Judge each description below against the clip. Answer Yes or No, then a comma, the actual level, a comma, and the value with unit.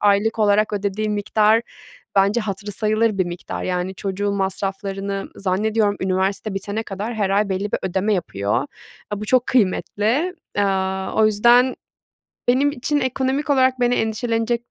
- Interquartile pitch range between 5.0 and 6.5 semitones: No, average, 2.8 semitones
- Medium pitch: No, high, 205 Hz